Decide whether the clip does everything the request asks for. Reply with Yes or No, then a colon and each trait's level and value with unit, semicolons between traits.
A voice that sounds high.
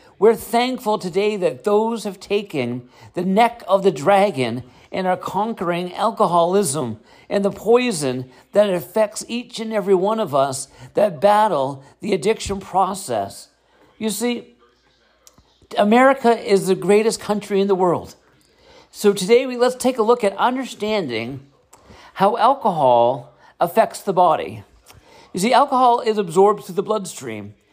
Yes: high, 200 Hz